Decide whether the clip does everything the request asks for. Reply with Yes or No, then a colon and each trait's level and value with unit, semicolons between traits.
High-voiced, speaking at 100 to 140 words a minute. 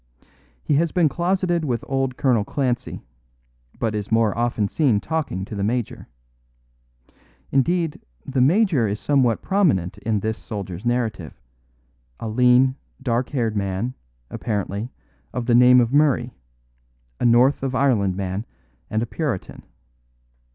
No: low, 120 Hz; slow, 135 wpm